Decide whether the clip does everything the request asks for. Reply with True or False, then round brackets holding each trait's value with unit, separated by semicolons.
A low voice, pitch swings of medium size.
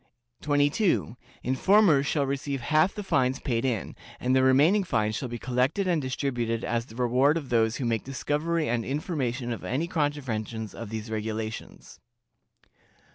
True (130 Hz; 4.2 semitones)